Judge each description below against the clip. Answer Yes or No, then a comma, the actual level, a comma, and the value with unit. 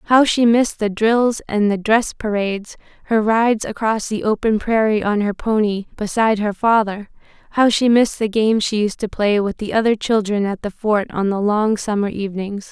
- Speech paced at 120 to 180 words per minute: No, average, 200 wpm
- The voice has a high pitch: Yes, high, 215 Hz